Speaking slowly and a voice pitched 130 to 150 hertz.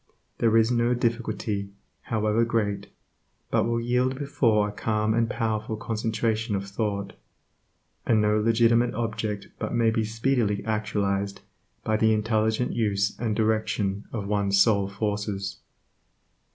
No: slow, 130 wpm; low, 110 Hz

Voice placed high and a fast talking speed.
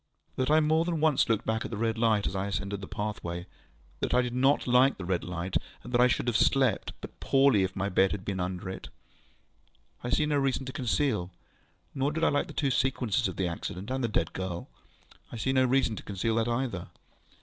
No: low, 115 Hz; fast, 230 wpm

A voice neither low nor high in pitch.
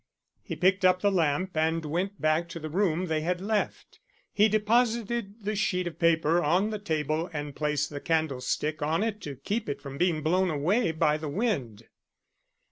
Yes: medium, 170 Hz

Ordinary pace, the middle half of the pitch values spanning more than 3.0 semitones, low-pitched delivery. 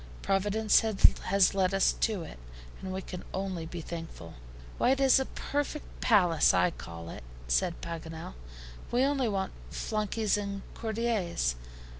No: average, 145 wpm; average, 4.6 semitones; high, 195 Hz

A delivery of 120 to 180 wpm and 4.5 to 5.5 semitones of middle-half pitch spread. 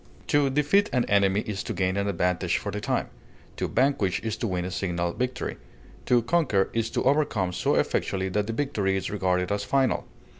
No: average, 195 wpm; average, 5.1 semitones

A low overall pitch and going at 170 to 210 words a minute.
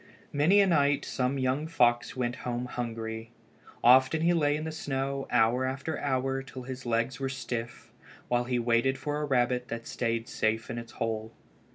Yes: low, 125 Hz; average, 180 wpm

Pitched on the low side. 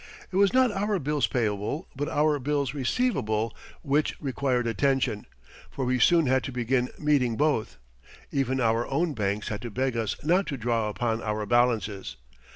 Yes: low, 130 Hz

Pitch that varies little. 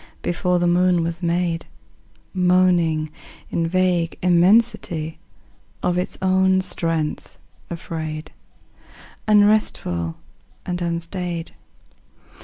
Yes: narrow, 1.8 semitones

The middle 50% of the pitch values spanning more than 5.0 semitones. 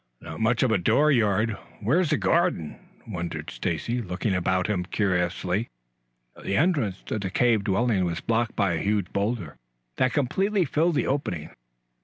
Yes: wide, 5.5 semitones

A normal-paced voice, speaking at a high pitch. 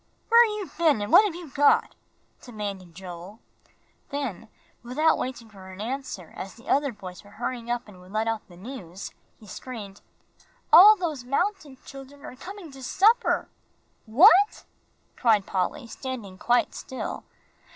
Yes: average, 150 wpm; high, 245 Hz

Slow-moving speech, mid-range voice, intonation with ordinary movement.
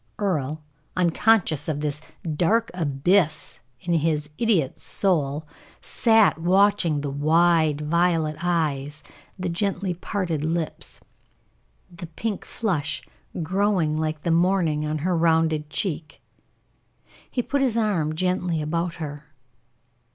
Yes: slow, 115 wpm; medium, 165 Hz; average, 3.4 semitones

